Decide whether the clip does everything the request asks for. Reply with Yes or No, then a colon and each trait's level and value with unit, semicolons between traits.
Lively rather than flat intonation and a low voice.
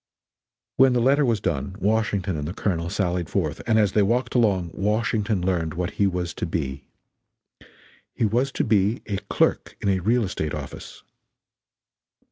No: average, 4.2 semitones; low, 100 Hz